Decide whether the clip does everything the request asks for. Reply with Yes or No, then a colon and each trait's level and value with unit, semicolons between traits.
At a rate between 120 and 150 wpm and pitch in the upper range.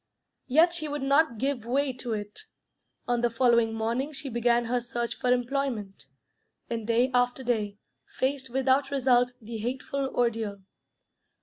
Yes: average, 145 wpm; high, 245 Hz